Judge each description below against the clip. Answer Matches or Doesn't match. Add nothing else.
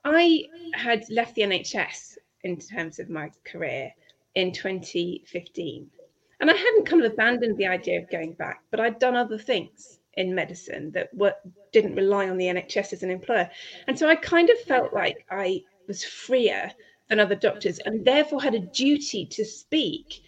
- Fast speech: Doesn't match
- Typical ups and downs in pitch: Doesn't match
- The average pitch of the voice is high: Matches